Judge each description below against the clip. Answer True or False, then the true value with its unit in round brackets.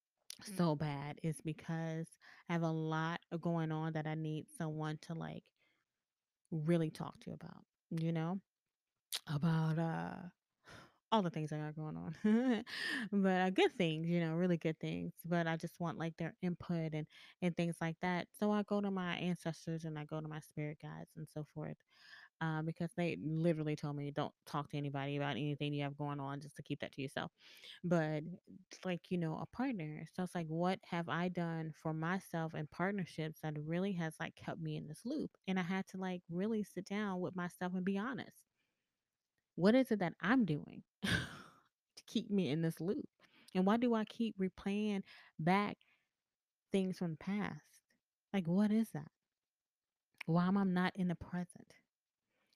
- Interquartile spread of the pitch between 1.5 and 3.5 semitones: True (3.2 semitones)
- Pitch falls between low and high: True (170 Hz)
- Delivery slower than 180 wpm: False (185 wpm)